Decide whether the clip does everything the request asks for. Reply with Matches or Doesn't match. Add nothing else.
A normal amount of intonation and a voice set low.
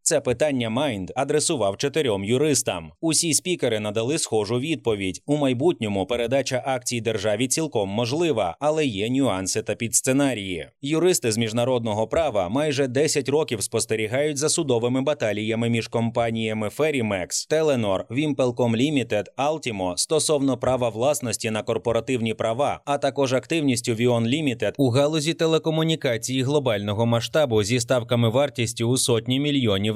Matches